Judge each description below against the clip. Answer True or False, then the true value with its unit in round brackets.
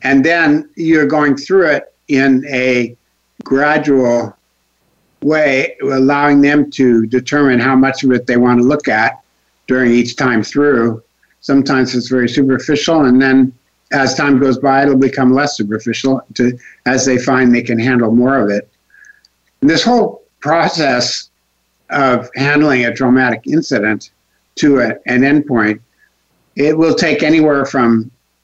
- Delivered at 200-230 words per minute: False (145 wpm)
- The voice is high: False (130 Hz)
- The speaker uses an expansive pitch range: False (3.0 semitones)